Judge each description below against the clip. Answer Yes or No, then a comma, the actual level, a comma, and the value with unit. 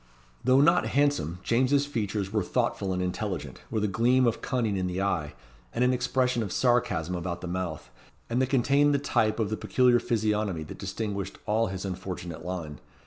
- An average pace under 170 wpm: No, average, 185 wpm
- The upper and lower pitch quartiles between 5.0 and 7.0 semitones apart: Yes, wide, 5.4 semitones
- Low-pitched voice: Yes, low, 105 Hz